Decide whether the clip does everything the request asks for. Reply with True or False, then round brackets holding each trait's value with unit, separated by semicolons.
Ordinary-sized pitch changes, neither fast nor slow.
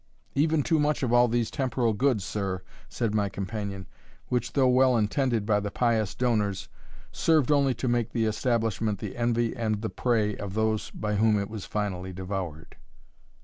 True (3.2 semitones; 175 wpm)